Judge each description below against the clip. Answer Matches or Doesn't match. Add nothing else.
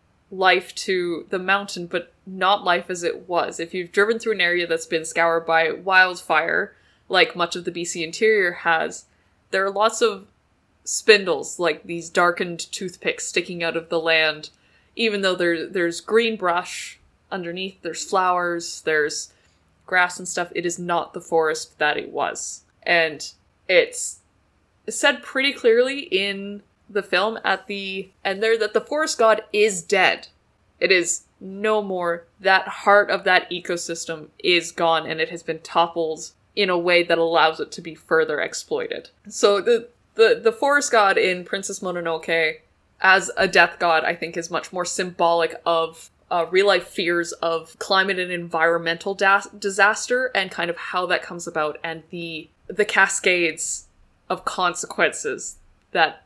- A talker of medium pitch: Matches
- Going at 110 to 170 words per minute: Matches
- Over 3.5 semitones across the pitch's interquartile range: Doesn't match